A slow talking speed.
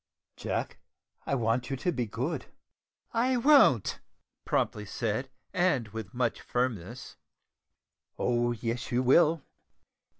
Yes: slow, 110 wpm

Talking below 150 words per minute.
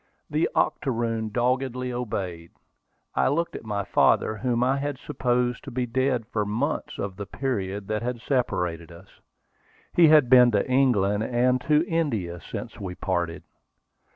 No: average, 155 wpm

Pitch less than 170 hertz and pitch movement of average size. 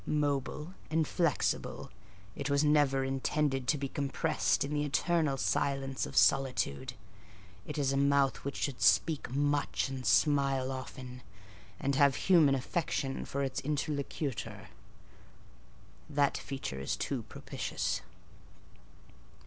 No: medium, 140 Hz; narrow, 1.7 semitones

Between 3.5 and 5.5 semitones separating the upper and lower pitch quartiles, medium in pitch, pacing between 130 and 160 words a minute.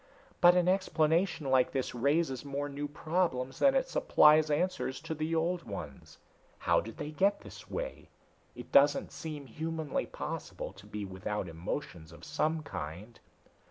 Yes: average, 4.6 semitones; medium, 150 Hz; average, 155 wpm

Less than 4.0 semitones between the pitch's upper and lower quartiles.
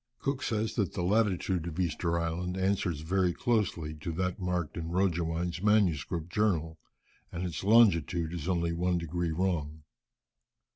Yes: narrow, 2.4 semitones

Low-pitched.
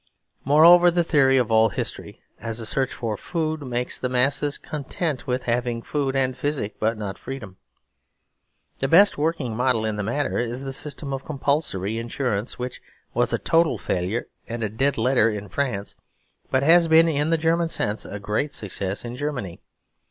Yes: low, 130 Hz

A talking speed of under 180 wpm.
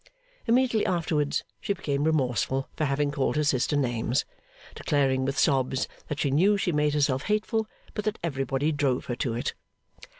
Yes: average, 165 wpm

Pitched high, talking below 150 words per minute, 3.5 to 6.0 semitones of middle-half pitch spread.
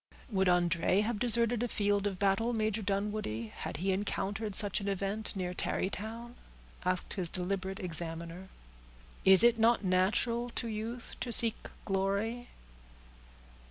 No: high, 200 Hz; slow, 135 wpm; average, 3.1 semitones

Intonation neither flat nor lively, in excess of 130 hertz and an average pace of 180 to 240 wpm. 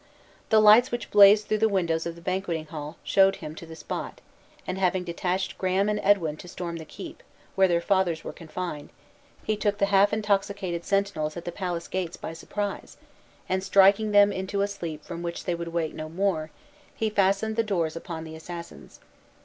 Yes: average, 3.1 semitones; medium, 185 Hz; average, 195 wpm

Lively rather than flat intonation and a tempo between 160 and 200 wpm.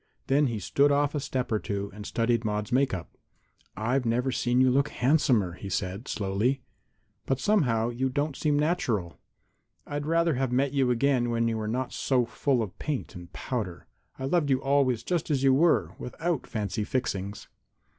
No: average, 4.2 semitones; average, 185 wpm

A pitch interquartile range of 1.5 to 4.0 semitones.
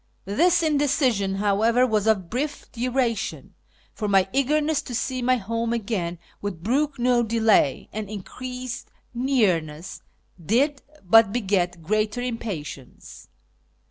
No: average, 4.4 semitones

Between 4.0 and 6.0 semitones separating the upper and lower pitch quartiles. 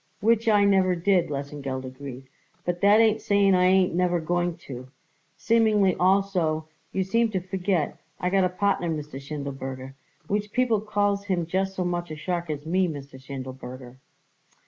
Yes: wide, 5.4 semitones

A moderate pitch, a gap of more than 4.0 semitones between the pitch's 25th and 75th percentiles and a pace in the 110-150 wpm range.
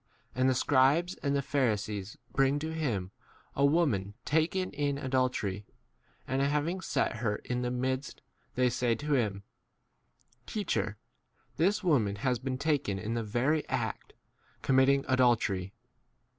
No: low, 130 Hz; average, 4.5 semitones; average, 145 wpm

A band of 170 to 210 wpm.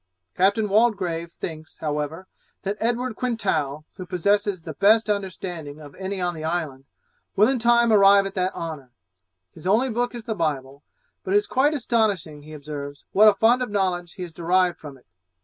Yes: average, 185 wpm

